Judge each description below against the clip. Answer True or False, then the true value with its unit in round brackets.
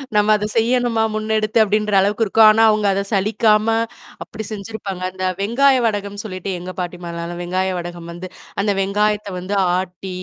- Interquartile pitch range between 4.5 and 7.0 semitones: False (2.7 semitones)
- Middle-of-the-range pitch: False (205 Hz)